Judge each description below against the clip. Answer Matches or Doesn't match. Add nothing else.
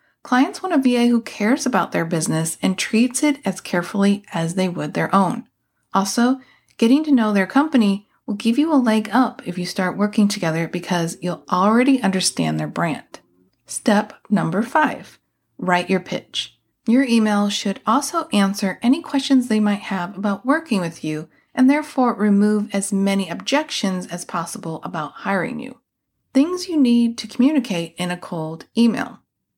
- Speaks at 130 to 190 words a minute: Matches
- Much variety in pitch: Matches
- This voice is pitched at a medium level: Doesn't match